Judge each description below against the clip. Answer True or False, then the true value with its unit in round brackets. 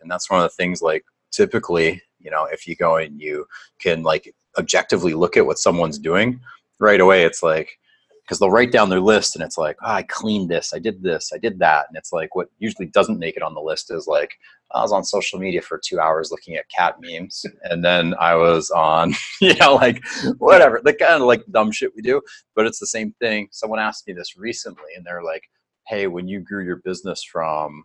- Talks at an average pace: False (235 wpm)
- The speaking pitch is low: True (90 Hz)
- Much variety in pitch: True (7.5 semitones)